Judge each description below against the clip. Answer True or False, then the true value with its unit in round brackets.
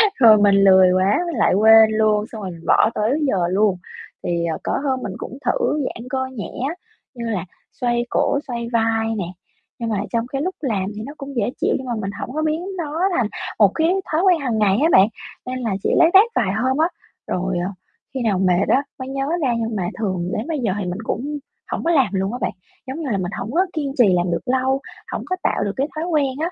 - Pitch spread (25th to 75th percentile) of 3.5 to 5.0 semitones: False (5.5 semitones)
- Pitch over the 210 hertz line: True (230 Hz)